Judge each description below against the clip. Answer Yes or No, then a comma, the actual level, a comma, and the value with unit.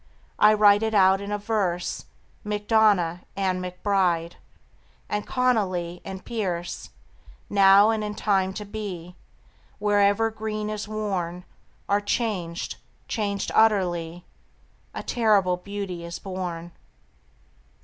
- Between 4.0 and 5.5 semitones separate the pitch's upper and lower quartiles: No, average, 2.8 semitones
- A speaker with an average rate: No, slow, 110 wpm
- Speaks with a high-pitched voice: Yes, high, 200 Hz